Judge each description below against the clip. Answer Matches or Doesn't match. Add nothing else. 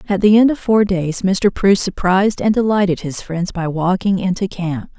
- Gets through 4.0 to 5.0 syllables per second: Matches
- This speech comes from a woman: Matches